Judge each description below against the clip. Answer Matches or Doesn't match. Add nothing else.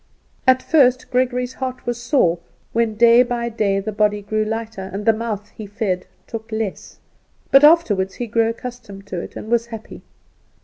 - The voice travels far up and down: Doesn't match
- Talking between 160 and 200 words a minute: Matches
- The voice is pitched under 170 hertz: Doesn't match